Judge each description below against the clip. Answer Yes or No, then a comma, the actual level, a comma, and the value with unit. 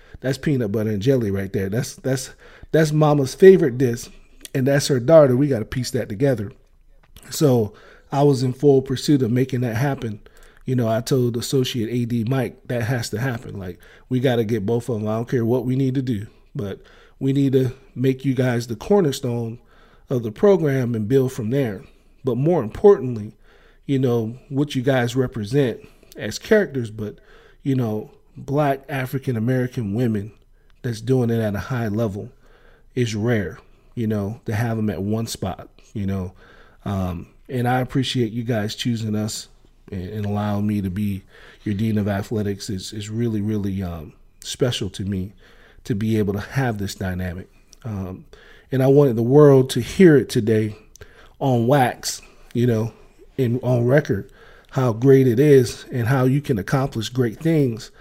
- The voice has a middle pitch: No, low, 120 Hz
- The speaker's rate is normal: Yes, average, 180 wpm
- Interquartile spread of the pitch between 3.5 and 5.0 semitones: Yes, average, 3.8 semitones